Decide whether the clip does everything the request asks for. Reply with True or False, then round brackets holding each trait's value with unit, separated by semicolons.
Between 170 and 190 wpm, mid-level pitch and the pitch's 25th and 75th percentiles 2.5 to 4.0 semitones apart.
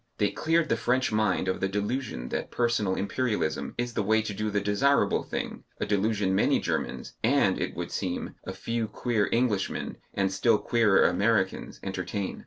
False (175 wpm; 105 Hz; 3.4 semitones)